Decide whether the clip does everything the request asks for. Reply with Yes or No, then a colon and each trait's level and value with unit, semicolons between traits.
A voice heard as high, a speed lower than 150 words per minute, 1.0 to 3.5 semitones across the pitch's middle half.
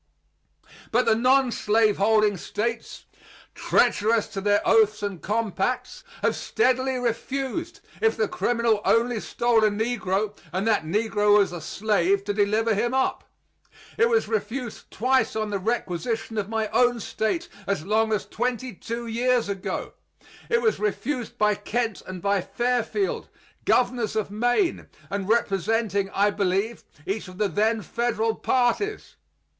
Yes: high, 225 Hz; average, 140 wpm; average, 3.0 semitones